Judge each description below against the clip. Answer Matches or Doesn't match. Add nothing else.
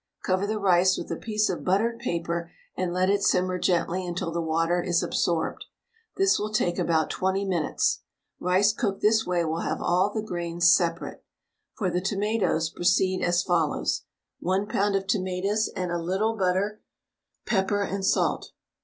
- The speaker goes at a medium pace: Matches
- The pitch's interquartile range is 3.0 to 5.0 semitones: Doesn't match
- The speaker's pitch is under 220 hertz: Matches